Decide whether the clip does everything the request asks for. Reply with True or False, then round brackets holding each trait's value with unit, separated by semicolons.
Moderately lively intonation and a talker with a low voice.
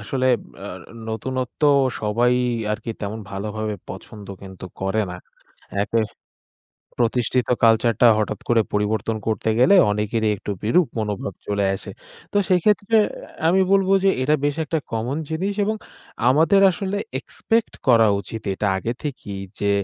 False (5.9 semitones; 115 Hz)